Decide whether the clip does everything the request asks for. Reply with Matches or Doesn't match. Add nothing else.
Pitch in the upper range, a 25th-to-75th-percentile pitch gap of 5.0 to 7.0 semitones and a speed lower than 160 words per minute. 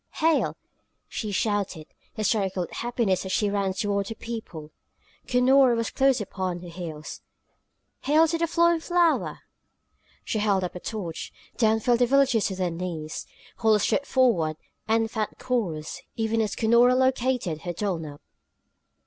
Matches